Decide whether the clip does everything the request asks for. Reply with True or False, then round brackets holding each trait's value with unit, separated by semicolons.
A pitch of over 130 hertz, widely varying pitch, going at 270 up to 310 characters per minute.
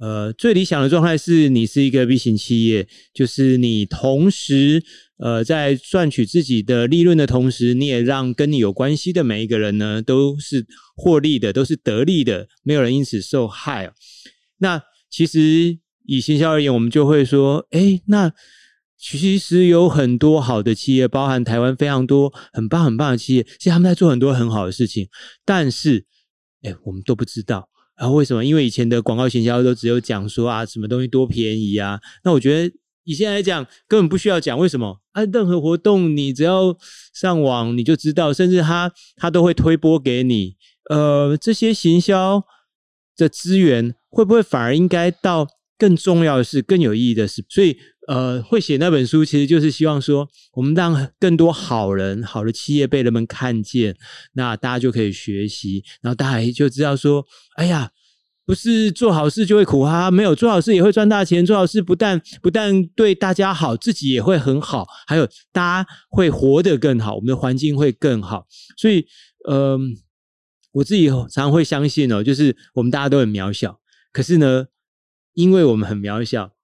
True (140 Hz; 6.2 semitones; 280 characters per minute)